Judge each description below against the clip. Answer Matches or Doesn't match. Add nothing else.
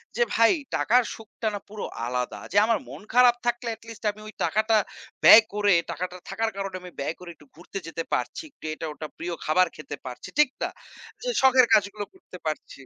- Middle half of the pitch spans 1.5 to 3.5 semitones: Doesn't match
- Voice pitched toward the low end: Doesn't match